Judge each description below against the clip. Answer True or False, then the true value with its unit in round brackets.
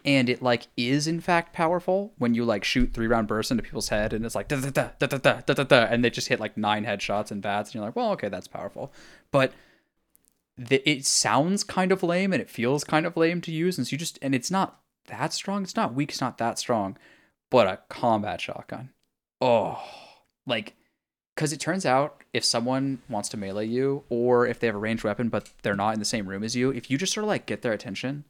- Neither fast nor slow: False (245 wpm)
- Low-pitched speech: True (130 Hz)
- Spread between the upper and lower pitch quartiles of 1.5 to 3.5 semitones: False (5.4 semitones)